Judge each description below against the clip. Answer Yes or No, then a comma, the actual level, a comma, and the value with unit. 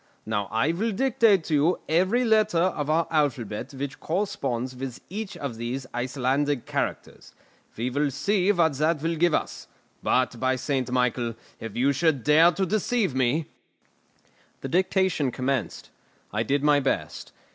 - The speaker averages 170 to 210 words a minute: No, average, 155 wpm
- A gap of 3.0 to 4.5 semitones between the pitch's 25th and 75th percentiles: No, wide, 5.4 semitones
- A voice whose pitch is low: No, medium, 145 Hz